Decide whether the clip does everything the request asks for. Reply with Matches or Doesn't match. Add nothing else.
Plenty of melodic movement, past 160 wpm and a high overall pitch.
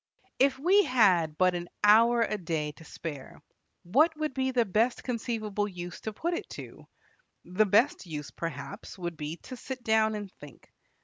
Matches